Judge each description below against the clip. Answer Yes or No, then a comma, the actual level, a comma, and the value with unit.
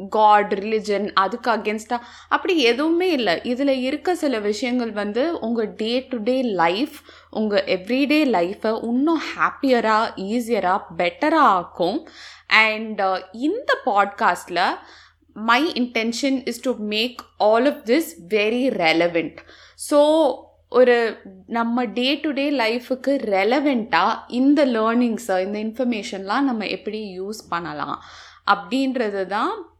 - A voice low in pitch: No, high, 235 Hz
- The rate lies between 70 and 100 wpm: No, average, 115 wpm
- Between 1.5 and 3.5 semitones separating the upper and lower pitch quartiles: No, average, 4.4 semitones